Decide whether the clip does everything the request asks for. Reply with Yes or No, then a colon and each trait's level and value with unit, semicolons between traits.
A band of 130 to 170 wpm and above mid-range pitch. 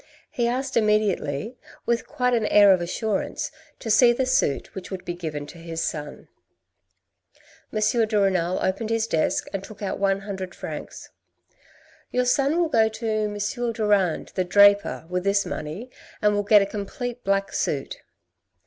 Yes: average, 165 wpm; high, 205 Hz